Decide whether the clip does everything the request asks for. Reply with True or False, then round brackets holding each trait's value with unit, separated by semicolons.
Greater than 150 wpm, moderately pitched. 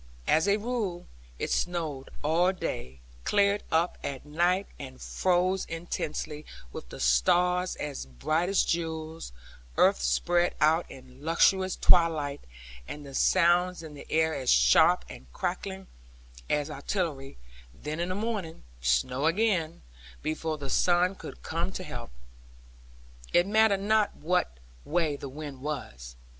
False (135 wpm; 160 Hz)